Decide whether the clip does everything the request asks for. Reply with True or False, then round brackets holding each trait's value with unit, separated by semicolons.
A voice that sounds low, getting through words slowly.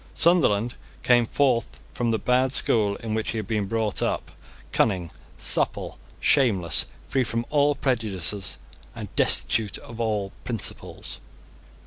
True (115 Hz; 130 wpm)